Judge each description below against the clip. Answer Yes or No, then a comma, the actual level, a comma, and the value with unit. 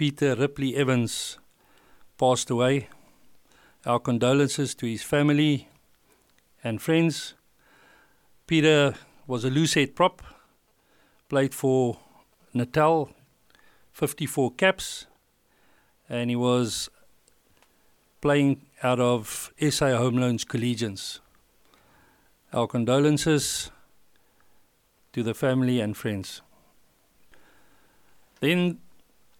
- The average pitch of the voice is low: Yes, low, 130 Hz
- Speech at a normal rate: No, slow, 80 wpm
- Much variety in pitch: No, average, 3.2 semitones